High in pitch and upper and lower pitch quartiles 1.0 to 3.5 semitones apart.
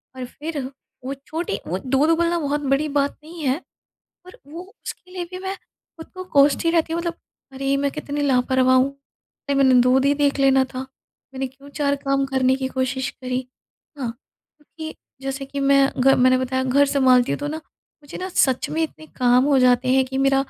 Yes: very high, 275 Hz; narrow, 2.4 semitones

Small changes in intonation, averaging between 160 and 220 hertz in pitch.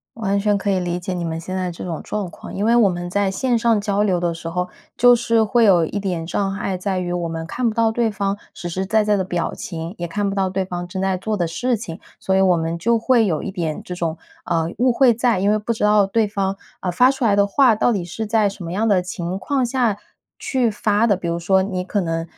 No: average, 3.7 semitones; high, 195 Hz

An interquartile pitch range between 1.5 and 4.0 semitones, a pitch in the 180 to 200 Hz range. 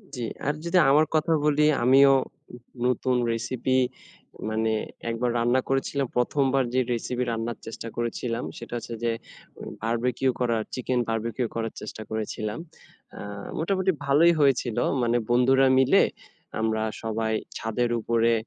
No: average, 2.8 semitones; low, 120 Hz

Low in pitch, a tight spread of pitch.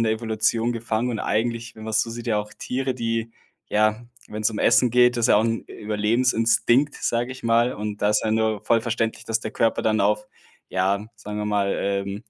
Yes: low, 110 Hz; narrow, 1.8 semitones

